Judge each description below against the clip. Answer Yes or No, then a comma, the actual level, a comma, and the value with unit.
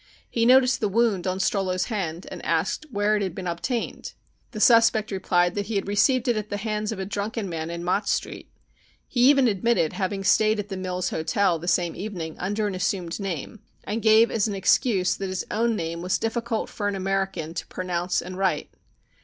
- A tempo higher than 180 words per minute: Yes, fast, 205 wpm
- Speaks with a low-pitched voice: No, high, 200 Hz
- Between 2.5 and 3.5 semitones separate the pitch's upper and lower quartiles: Yes, average, 3.2 semitones